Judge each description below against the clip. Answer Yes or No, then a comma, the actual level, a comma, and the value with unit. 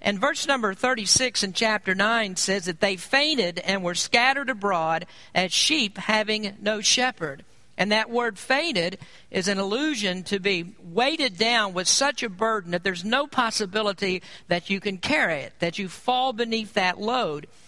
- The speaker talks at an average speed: Yes, average, 170 wpm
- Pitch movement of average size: Yes, average, 4.3 semitones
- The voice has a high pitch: Yes, high, 205 Hz